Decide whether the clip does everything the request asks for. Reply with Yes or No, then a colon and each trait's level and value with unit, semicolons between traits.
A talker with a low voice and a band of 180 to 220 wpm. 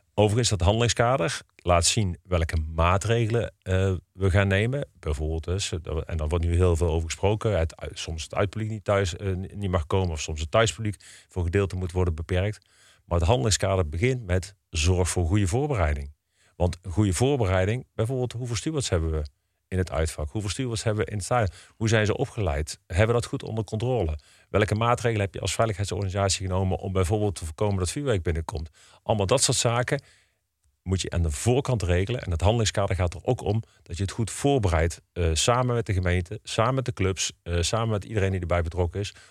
Yes: very low, 95 Hz; average, 195 wpm